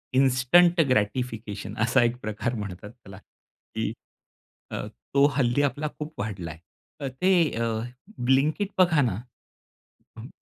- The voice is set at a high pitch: No, low, 125 Hz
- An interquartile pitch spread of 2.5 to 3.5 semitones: No, average, 5.2 semitones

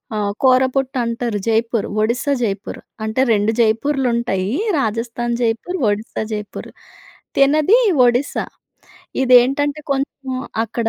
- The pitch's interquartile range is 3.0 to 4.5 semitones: Yes, average, 3.5 semitones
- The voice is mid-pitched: No, high, 240 Hz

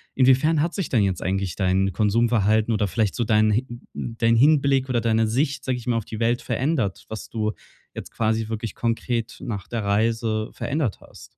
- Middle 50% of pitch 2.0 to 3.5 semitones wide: Yes, average, 2.7 semitones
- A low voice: Yes, low, 115 Hz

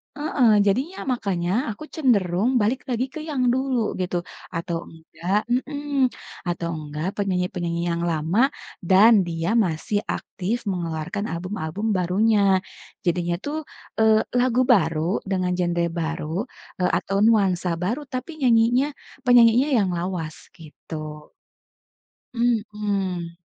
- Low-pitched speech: No, high, 195 Hz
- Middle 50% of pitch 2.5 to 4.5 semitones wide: No, wide, 5.4 semitones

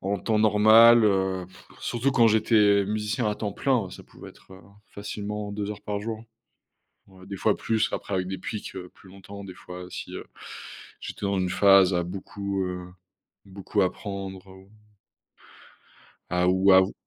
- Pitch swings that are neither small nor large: No, narrow, 2.0 semitones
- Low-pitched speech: Yes, low, 100 Hz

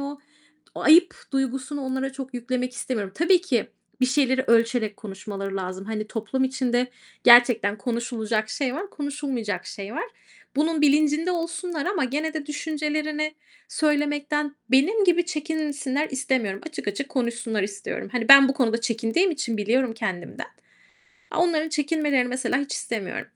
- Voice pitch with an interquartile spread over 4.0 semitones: Yes, average, 4.8 semitones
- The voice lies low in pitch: No, very high, 265 Hz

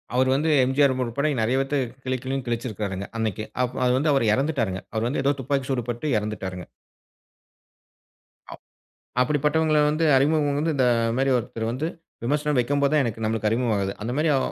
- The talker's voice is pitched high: No, low, 130 Hz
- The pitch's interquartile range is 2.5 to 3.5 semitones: No, average, 4.2 semitones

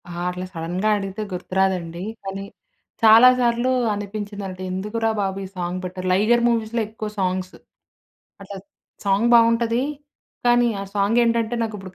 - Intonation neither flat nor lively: Yes, average, 3.5 semitones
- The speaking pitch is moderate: No, high, 205 Hz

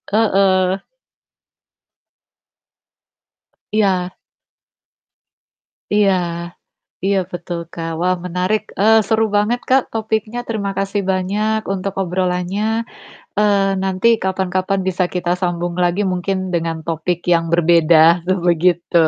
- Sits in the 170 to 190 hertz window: Yes, medium, 185 Hz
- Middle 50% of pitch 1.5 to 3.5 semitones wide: Yes, narrow, 2.6 semitones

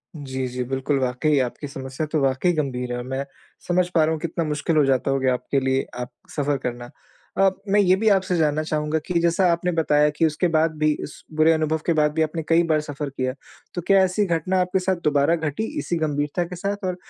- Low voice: No, medium, 155 Hz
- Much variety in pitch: No, average, 3.9 semitones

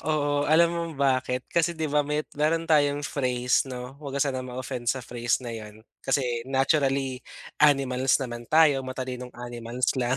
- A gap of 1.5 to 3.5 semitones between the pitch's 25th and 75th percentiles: Yes, narrow, 2.6 semitones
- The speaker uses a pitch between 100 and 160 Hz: Yes, low, 135 Hz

